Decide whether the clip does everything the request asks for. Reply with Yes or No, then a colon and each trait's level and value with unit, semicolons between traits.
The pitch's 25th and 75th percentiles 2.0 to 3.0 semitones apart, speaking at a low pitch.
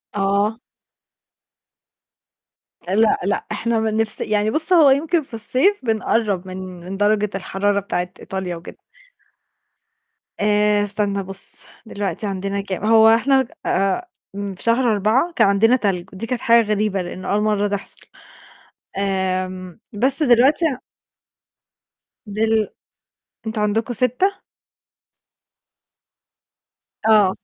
No: average, 2.7 semitones; high, 210 Hz